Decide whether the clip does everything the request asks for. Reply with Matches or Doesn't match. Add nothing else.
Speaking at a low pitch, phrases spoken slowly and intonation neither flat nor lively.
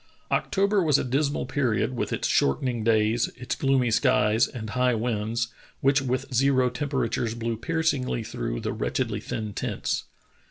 Doesn't match